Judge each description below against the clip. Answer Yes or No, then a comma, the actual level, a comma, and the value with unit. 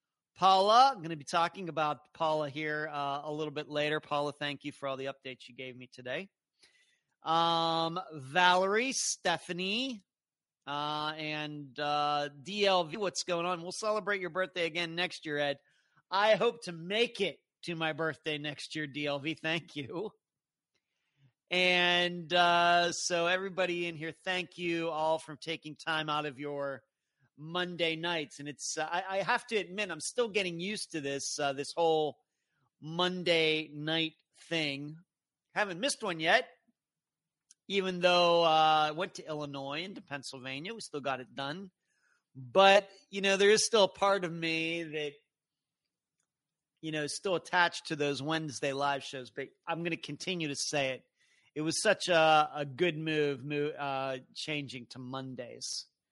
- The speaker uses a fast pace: No, average, 160 wpm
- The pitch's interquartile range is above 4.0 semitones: No, average, 3.6 semitones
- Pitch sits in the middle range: Yes, medium, 160 Hz